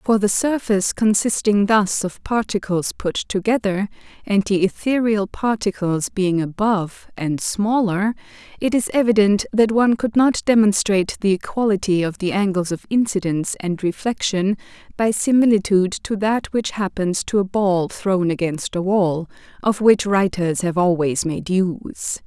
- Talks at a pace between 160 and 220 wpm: No, average, 145 wpm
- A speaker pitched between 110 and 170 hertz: No, high, 200 Hz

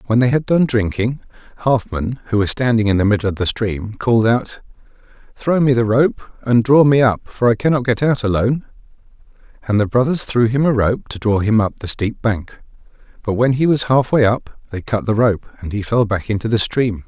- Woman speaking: No, male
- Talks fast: Yes, fast, 220 wpm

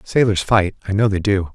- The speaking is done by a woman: No, male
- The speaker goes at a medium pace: No, fast, 235 wpm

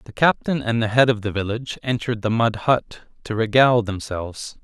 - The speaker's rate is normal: Yes, average, 195 wpm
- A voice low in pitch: Yes, low, 115 Hz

